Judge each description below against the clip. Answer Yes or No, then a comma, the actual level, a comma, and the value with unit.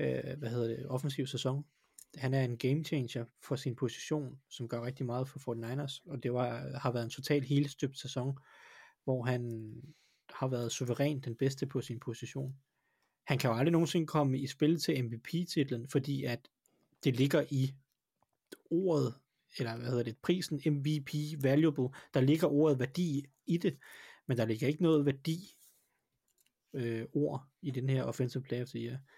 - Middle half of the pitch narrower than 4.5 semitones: Yes, average, 2.9 semitones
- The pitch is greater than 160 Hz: No, low, 135 Hz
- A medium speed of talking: Yes, average, 165 wpm